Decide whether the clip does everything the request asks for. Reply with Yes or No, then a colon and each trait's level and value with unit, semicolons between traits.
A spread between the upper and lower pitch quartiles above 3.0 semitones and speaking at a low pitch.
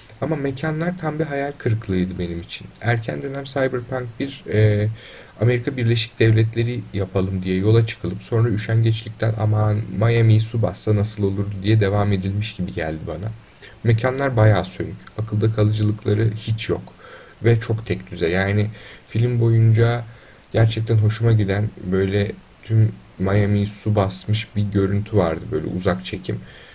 No: narrow, 2.6 semitones; low, 110 Hz